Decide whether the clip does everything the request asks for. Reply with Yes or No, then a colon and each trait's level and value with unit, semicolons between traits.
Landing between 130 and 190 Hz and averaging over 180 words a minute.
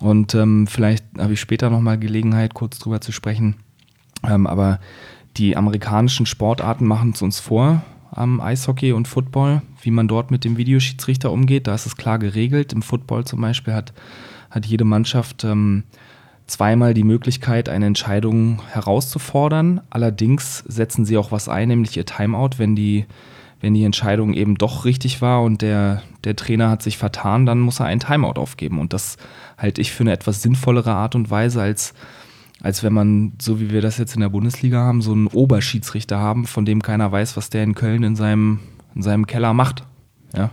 No: low, 115 Hz; fast, 190 wpm